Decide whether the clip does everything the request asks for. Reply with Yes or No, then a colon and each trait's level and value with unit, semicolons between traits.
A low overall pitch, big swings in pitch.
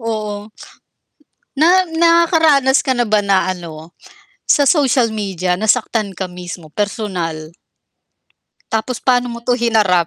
No: high, 220 Hz; wide, 5.7 semitones